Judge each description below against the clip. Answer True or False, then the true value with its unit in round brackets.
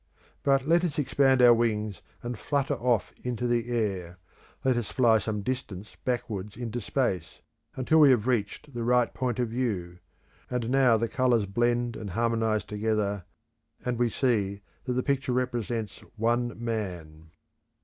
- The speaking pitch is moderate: False (120 Hz)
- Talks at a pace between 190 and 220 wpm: False (155 wpm)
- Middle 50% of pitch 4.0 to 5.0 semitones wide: False (3.0 semitones)